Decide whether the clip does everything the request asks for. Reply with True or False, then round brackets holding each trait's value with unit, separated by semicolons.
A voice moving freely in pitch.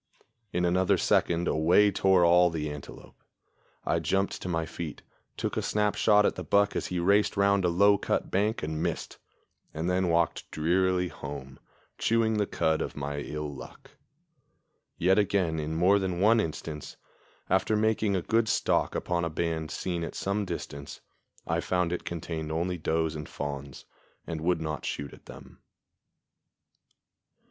False (3.7 semitones)